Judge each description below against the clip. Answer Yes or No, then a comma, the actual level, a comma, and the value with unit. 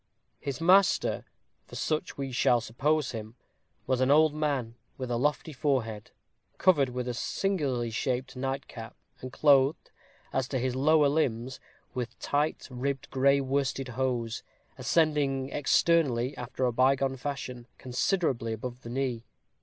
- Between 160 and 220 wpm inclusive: No, average, 140 wpm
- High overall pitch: No, low, 130 Hz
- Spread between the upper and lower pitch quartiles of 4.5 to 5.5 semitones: No, average, 2.7 semitones